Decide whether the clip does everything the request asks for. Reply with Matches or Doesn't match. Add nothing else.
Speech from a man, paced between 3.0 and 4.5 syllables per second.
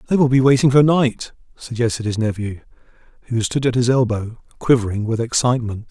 Doesn't match